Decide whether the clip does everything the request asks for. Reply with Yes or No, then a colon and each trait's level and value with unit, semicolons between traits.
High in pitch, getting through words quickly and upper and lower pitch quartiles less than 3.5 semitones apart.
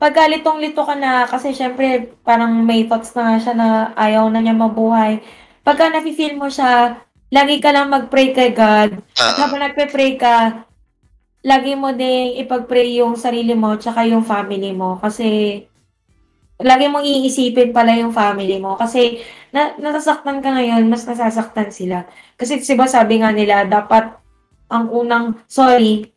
No: high, 235 Hz; average, 155 wpm; average, 3.1 semitones